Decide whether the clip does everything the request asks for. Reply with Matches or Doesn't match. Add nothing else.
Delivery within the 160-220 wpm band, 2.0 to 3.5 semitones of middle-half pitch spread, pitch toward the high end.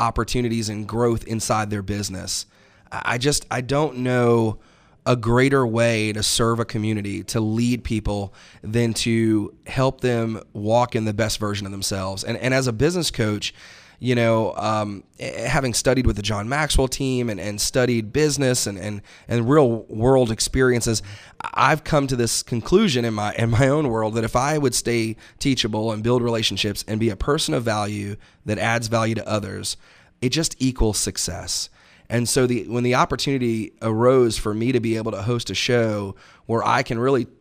Doesn't match